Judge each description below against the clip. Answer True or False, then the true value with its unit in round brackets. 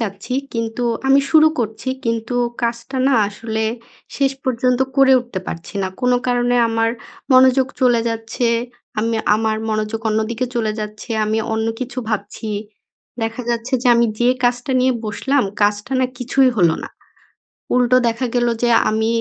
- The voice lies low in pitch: False (235 Hz)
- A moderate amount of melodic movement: False (2.3 semitones)